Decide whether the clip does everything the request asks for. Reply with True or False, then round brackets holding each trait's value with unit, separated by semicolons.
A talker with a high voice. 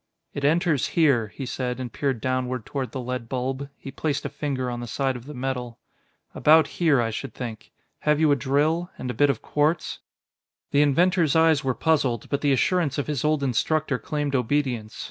False (140 Hz)